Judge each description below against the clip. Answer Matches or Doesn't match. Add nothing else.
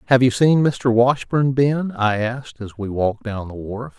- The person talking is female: Doesn't match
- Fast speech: Matches